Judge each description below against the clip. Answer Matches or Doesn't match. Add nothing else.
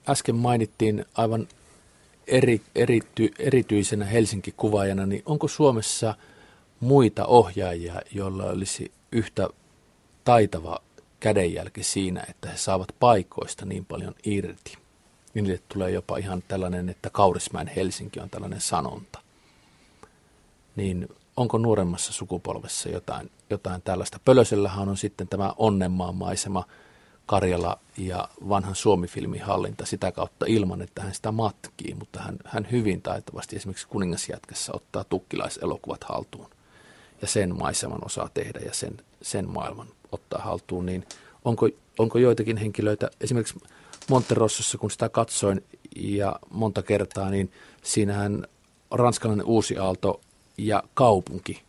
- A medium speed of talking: Matches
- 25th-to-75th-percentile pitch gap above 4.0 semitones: Doesn't match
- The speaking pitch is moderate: Doesn't match